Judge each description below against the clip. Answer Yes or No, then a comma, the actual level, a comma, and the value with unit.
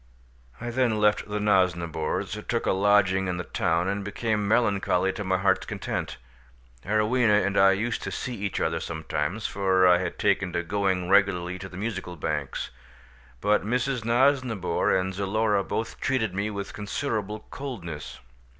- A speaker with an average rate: Yes, average, 160 wpm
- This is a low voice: Yes, low, 100 Hz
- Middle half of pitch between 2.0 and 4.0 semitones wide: Yes, average, 2.7 semitones